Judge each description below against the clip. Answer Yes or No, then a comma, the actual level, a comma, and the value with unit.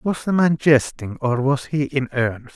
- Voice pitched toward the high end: No, low, 135 Hz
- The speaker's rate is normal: No, fast, 210 wpm